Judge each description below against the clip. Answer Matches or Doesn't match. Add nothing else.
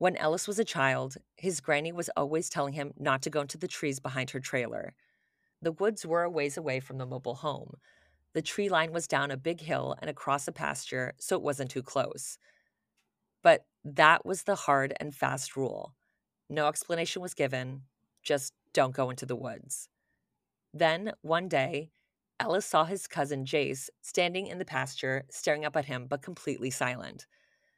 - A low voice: Doesn't match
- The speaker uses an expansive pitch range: Doesn't match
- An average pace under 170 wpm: Doesn't match